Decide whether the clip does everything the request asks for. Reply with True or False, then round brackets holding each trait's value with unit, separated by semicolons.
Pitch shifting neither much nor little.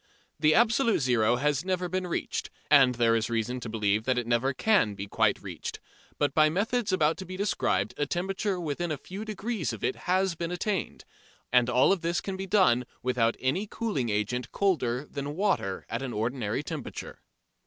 False (7.7 semitones)